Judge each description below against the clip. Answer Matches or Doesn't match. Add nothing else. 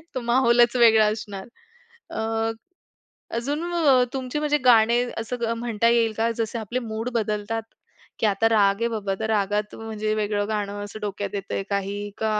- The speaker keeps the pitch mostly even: Matches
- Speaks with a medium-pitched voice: Doesn't match